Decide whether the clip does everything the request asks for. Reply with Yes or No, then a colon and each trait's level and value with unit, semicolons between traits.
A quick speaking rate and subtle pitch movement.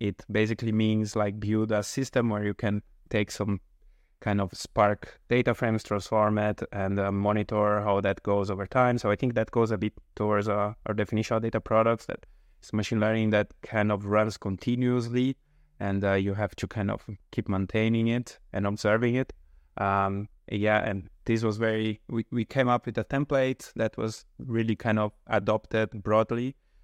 No: average, 185 wpm; narrow, 1.9 semitones